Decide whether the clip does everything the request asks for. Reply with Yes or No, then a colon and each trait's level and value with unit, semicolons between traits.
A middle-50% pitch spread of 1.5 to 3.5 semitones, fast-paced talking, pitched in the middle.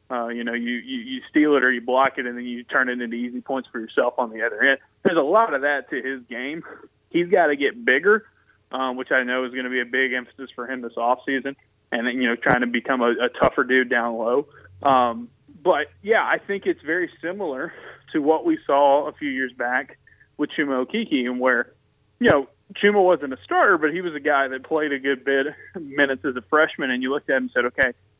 No: narrow, 2.5 semitones; fast, 250 wpm; low, 130 Hz